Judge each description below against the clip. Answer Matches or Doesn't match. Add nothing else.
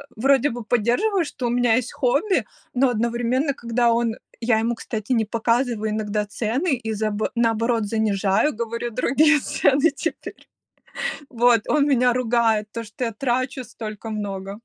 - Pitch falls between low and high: Doesn't match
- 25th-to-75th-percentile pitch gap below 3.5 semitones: Matches